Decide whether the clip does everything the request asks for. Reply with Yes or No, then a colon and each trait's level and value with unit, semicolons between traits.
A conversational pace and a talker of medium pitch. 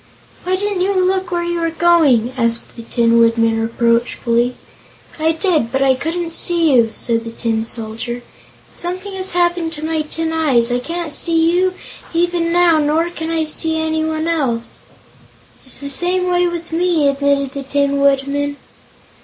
No: average, 165 wpm; very high, 315 Hz